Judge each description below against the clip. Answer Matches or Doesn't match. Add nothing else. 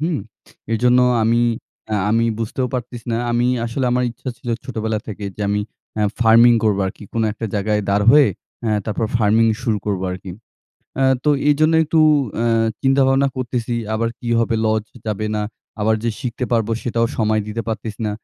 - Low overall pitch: Matches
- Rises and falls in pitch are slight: Matches